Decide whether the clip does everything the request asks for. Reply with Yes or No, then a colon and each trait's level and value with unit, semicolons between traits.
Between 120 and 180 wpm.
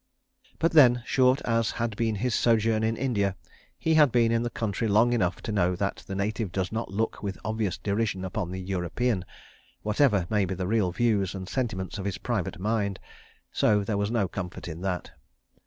No: average, 190 wpm